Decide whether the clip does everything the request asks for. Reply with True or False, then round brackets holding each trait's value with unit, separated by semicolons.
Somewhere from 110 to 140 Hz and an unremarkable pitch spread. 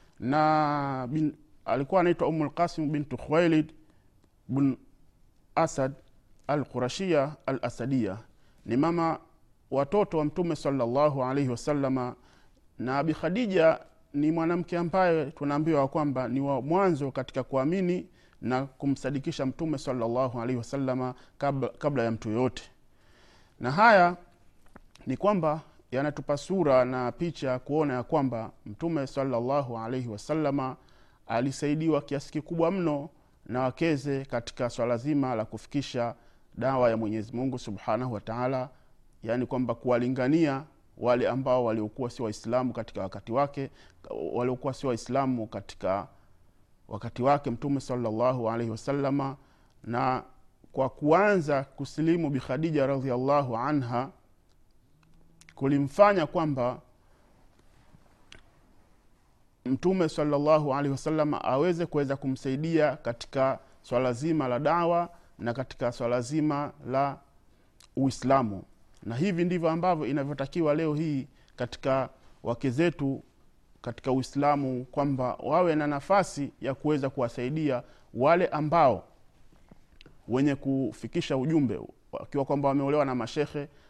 True (135 Hz; 3.4 semitones)